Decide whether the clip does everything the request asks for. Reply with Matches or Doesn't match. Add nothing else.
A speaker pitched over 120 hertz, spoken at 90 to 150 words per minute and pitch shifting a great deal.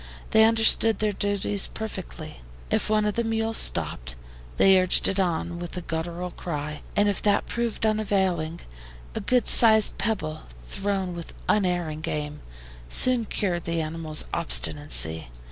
Doesn't match